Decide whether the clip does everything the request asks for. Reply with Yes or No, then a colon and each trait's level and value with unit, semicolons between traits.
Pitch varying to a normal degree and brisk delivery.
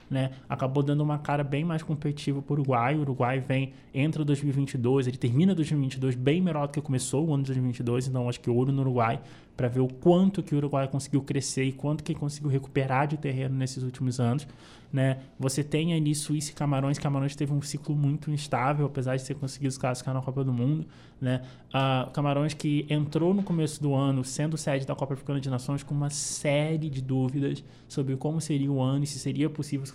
No: narrow, 2.0 semitones; fast, 215 wpm